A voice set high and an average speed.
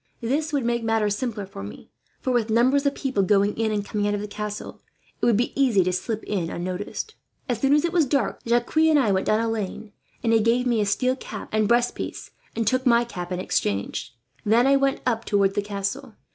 No: high, 225 Hz; fast, 235 wpm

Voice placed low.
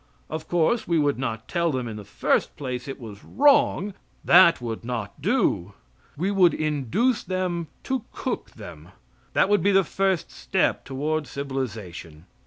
No: medium, 150 Hz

